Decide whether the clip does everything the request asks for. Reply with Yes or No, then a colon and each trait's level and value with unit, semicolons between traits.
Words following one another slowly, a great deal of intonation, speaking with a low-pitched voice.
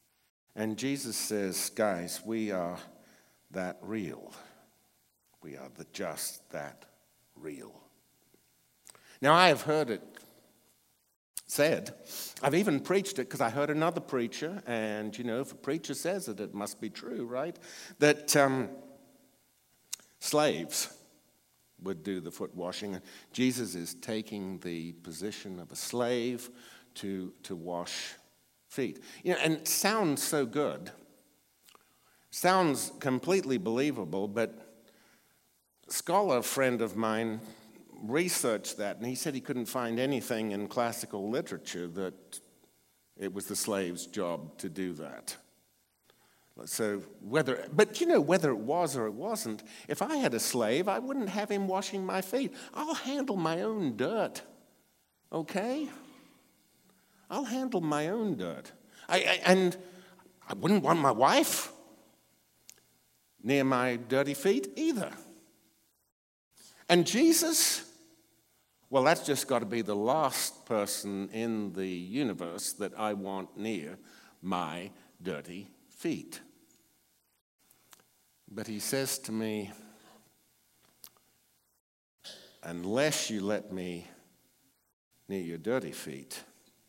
Yes: slow, 125 wpm; wide, 8.4 semitones; low, 115 Hz